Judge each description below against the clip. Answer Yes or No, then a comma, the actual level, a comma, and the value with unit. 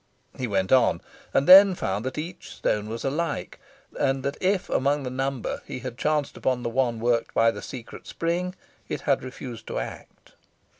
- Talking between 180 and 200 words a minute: Yes, average, 185 wpm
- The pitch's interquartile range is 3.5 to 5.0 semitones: Yes, average, 4.3 semitones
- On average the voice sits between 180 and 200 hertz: No, low, 130 Hz